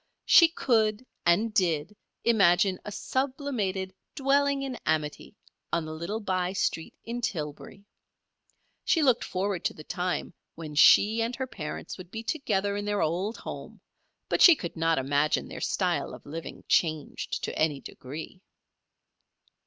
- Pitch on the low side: No, high, 190 Hz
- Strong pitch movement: Yes, wide, 5.9 semitones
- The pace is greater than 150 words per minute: No, average, 145 wpm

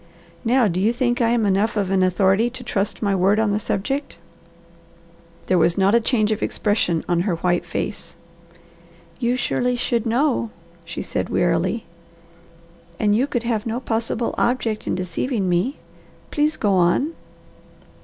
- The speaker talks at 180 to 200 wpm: No, average, 160 wpm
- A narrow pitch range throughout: No, average, 4.2 semitones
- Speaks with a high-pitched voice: Yes, high, 215 Hz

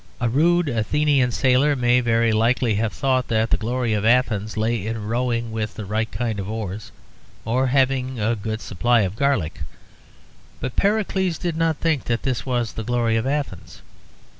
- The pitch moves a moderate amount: Yes, average, 3.2 semitones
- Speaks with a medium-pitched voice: No, low, 120 Hz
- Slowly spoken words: No, average, 175 wpm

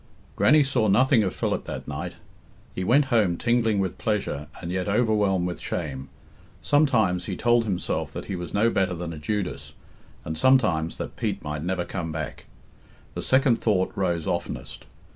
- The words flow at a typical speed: Yes, average, 170 wpm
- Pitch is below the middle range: Yes, very low, 95 Hz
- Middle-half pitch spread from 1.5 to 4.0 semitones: No, average, 5.0 semitones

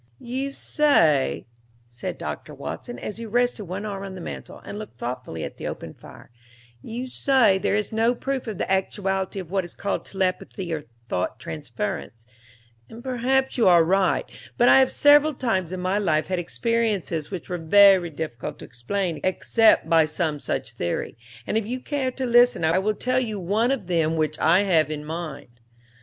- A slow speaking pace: No, average, 185 wpm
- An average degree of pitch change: No, wide, 6.4 semitones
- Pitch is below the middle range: No, high, 190 Hz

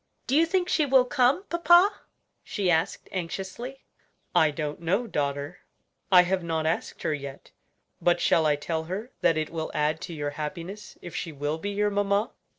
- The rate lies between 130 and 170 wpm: No, average, 180 wpm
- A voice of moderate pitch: Yes, medium, 175 Hz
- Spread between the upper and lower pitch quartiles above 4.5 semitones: Yes, average, 5.3 semitones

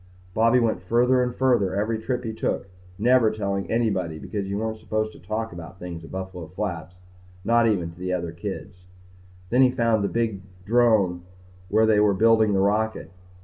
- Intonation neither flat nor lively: Yes, average, 3.5 semitones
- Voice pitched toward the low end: Yes, low, 105 Hz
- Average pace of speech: Yes, average, 185 wpm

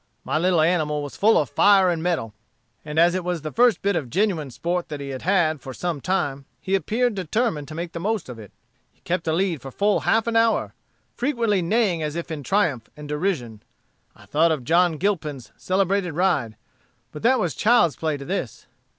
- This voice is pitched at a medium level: Yes, medium, 170 Hz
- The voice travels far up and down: No, average, 4.8 semitones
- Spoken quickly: Yes, fast, 210 wpm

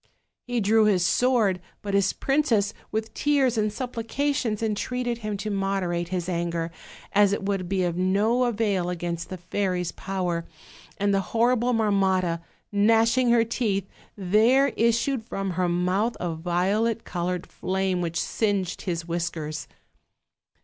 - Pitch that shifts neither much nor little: Yes, average, 4.2 semitones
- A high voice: Yes, high, 200 Hz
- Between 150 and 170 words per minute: No, average, 140 wpm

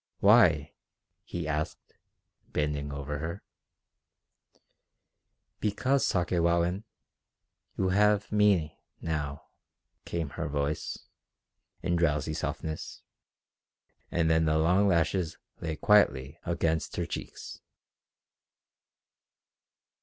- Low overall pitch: Yes, very low, 80 Hz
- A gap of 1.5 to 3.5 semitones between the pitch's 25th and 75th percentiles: Yes, average, 3.2 semitones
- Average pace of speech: No, slow, 85 wpm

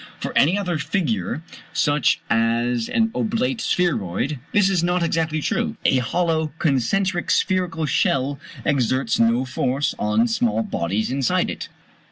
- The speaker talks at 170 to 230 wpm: No, slow, 135 wpm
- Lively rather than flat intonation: Yes, wide, 6.9 semitones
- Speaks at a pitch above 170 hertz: No, medium, 145 Hz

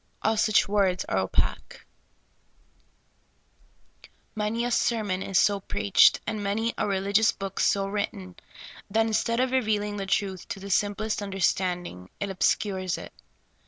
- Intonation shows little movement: Yes, narrow, 2.0 semitones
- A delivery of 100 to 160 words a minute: Yes, average, 140 wpm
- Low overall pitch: No, high, 200 Hz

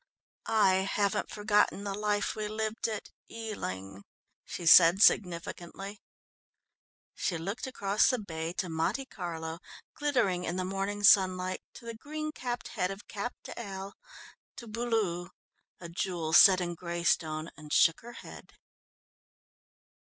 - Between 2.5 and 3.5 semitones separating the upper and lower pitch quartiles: No, average, 4.0 semitones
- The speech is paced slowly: Yes, slow, 130 wpm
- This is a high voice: Yes, high, 195 Hz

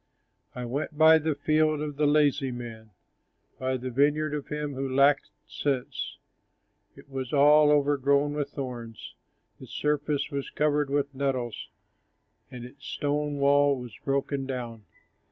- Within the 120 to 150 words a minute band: Yes, average, 140 wpm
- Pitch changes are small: Yes, narrow, 2.2 semitones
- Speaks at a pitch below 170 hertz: Yes, medium, 140 Hz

